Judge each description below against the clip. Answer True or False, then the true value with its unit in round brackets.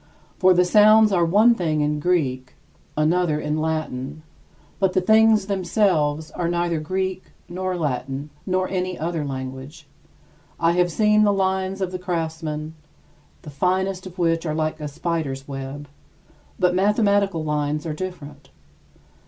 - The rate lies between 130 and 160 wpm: True (145 wpm)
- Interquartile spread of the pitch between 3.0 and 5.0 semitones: True (3.7 semitones)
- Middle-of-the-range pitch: True (170 Hz)